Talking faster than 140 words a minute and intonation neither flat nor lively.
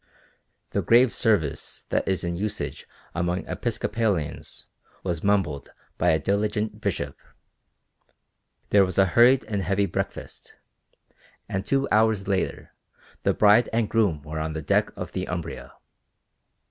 No: slow, 135 wpm; average, 3.9 semitones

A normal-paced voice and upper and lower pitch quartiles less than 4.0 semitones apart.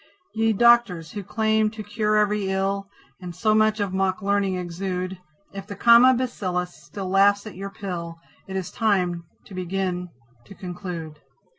Yes: average, 160 wpm; average, 2.8 semitones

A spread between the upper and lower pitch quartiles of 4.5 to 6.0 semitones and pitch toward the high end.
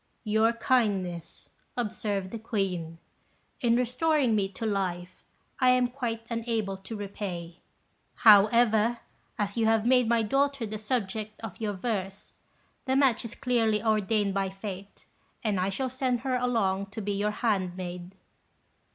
No: average, 3.4 semitones; high, 215 Hz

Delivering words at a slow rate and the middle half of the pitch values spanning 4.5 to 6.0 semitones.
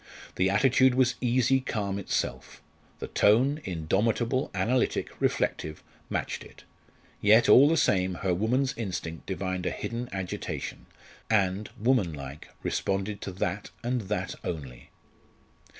Yes: slow, 125 wpm; average, 5.1 semitones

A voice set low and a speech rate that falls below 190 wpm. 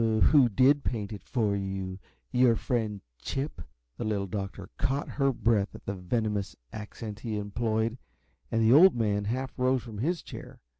Yes: low, 110 Hz; average, 165 wpm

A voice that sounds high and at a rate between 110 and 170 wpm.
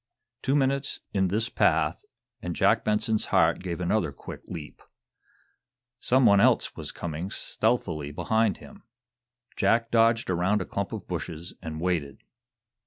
No: low, 100 Hz; average, 140 wpm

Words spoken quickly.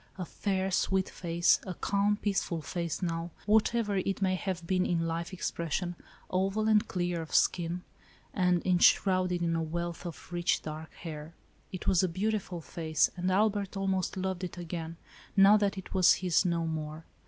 No: average, 170 wpm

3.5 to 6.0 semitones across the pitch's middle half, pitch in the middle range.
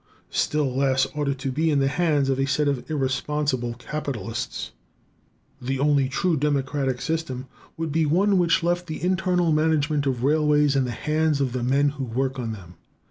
No: average, 3.0 semitones; medium, 145 Hz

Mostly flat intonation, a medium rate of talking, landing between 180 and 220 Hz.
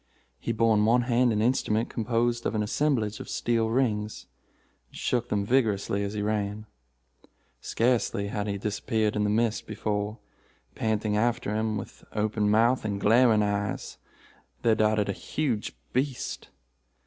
No: narrow, 2.1 semitones; average, 150 wpm; low, 110 Hz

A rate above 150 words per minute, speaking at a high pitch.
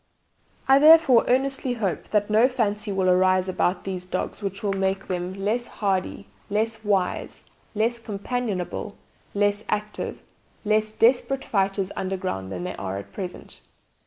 No: average, 145 wpm; high, 205 Hz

